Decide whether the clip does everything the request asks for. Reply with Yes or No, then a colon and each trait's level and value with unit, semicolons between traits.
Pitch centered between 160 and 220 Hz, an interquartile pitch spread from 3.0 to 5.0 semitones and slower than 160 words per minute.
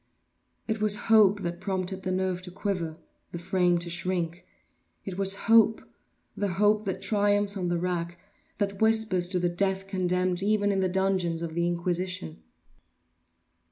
No: medium, 185 Hz; narrow, 2.4 semitones; average, 145 wpm